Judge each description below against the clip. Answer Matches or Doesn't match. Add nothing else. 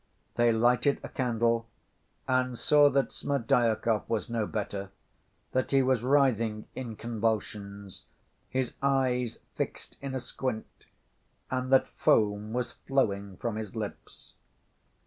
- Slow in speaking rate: Matches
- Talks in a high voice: Doesn't match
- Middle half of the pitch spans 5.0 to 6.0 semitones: Doesn't match